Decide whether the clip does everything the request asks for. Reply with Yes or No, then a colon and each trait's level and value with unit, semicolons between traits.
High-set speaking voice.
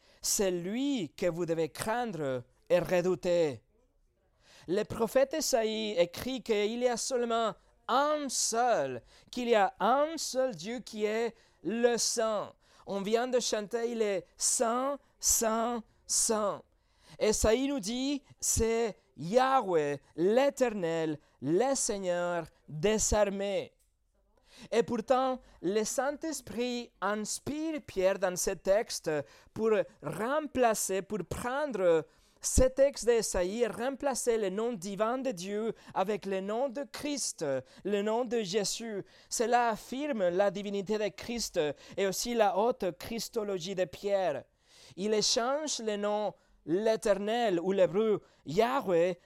Yes: high, 220 Hz